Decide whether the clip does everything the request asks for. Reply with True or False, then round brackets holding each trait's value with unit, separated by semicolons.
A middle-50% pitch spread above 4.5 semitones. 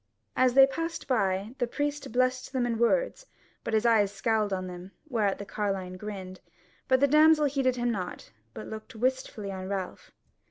True (5.0 semitones)